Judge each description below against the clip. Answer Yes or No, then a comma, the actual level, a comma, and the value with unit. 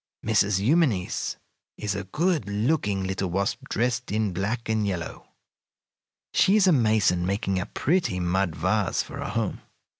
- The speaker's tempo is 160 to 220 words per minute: No, average, 150 wpm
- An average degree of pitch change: Yes, average, 4.4 semitones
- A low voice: Yes, low, 105 Hz